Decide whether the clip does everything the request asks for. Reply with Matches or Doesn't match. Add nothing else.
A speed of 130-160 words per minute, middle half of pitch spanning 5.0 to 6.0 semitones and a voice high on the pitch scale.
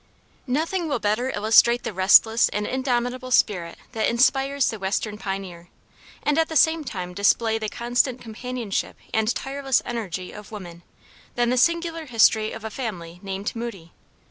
Doesn't match